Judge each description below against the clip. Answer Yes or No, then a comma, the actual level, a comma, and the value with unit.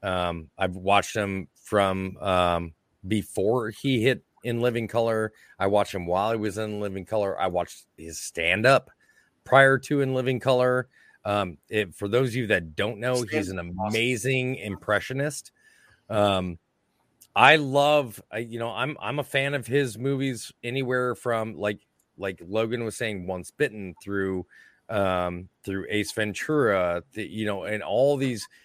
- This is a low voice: Yes, low, 110 Hz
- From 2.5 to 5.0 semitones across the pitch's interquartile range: Yes, average, 4.6 semitones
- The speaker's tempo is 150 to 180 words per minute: Yes, average, 160 wpm